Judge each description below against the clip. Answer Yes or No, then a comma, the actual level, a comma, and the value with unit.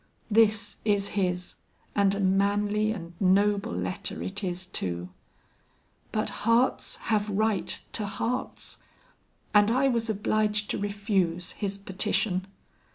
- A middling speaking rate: No, slow, 120 wpm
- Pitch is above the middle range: Yes, high, 205 Hz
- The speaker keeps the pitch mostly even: Yes, narrow, 2.0 semitones